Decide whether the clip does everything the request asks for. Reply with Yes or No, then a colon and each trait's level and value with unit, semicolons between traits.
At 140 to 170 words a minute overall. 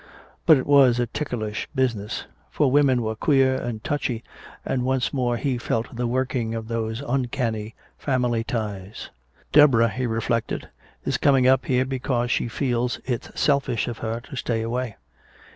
Yes: average, 160 wpm